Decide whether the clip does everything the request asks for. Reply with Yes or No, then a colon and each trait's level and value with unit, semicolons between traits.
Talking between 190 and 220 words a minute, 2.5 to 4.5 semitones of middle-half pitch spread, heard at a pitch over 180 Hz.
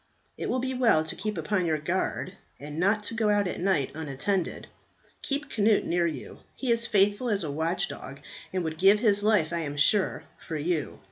No: average, 200 wpm; average, 4.9 semitones; high, 190 Hz